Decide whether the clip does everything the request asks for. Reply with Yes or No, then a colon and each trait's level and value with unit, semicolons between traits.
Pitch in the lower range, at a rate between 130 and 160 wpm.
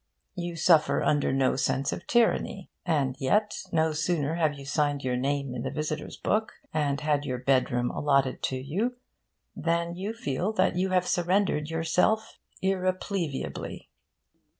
No: medium, 155 Hz; average, 150 wpm